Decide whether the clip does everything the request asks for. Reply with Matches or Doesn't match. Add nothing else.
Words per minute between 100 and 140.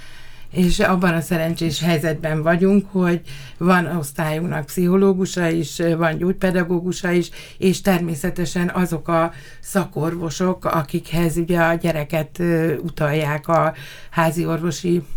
Matches